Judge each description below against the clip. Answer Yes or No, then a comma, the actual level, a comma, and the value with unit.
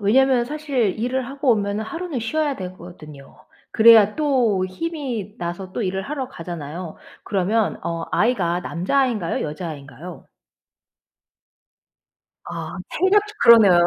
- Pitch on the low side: No, high, 210 Hz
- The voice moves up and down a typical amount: No, wide, 6.8 semitones